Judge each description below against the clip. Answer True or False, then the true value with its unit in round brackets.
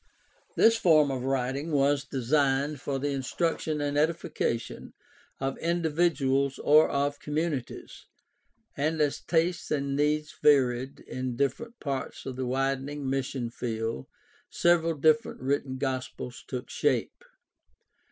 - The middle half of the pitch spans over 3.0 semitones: False (2.6 semitones)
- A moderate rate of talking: False (125 wpm)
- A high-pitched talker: False (140 Hz)